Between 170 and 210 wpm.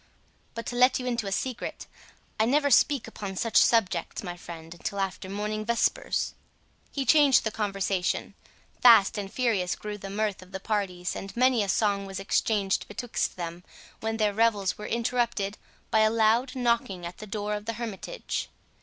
Yes: average, 175 wpm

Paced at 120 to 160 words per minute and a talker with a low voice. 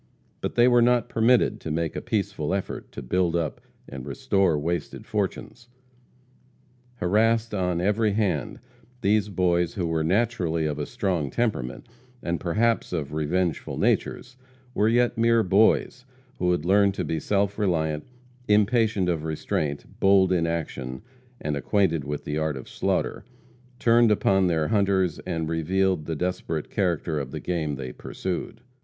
Yes: average, 150 wpm; very low, 90 Hz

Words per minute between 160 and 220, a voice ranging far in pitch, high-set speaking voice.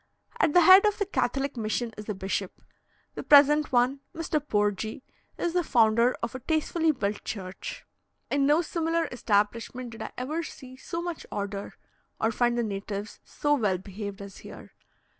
Yes: average, 170 wpm; wide, 6.4 semitones; high, 245 Hz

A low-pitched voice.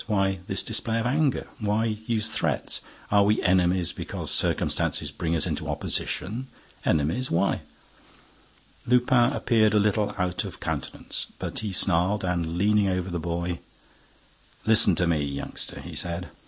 Yes: low, 100 Hz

